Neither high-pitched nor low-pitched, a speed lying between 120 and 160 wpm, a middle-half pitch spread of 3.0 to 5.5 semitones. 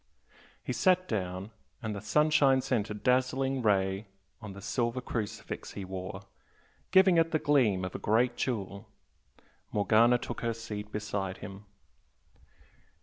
No: low, 110 Hz; average, 140 wpm; average, 4.4 semitones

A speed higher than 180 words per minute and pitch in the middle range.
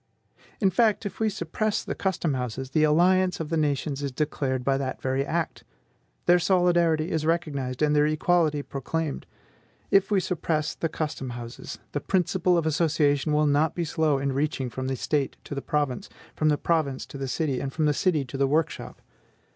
Yes: average, 190 wpm; medium, 155 Hz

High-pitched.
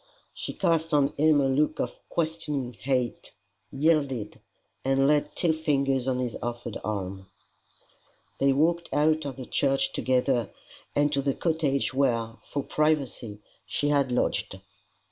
No: medium, 140 Hz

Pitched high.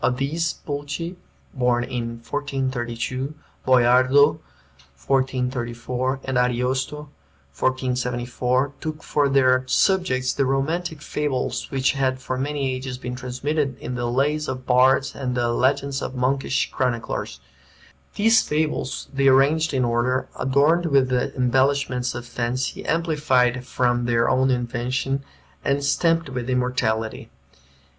No: low, 130 Hz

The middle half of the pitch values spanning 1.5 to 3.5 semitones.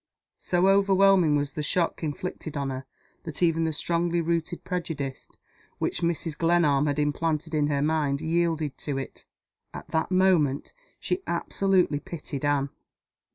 Yes: average, 3.0 semitones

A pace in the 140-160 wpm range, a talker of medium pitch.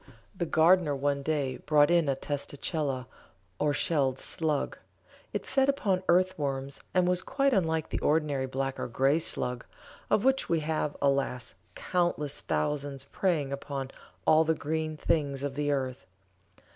Yes: average, 150 wpm; medium, 150 Hz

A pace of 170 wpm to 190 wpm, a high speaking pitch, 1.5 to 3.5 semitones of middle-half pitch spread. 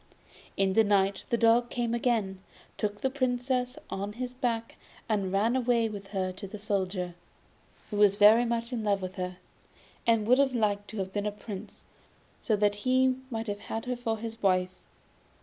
Yes: average, 185 wpm; high, 215 Hz; average, 3.2 semitones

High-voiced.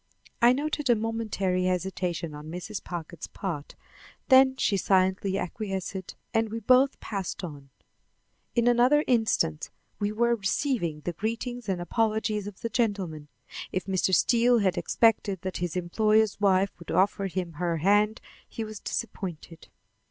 Yes: high, 200 Hz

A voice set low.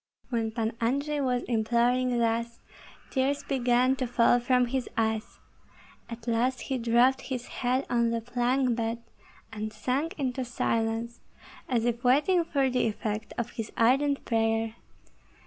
No: high, 240 Hz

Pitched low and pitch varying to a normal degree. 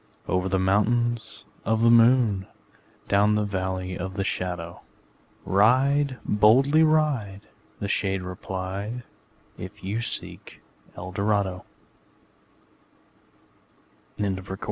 Yes: low, 100 Hz; average, 3.9 semitones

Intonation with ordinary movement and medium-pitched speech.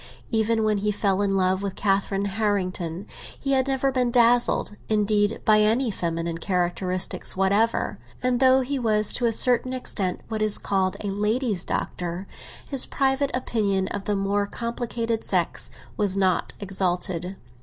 No: average, 3.5 semitones; high, 205 Hz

